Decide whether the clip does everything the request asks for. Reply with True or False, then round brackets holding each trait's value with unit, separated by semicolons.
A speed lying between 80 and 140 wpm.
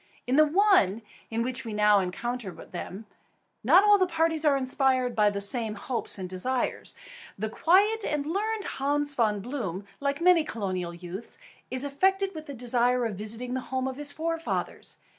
False (175 wpm)